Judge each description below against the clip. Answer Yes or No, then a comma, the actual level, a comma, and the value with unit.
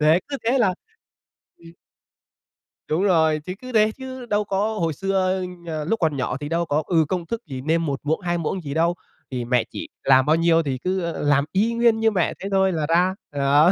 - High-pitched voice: No, medium, 170 Hz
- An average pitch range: Yes, average, 4.2 semitones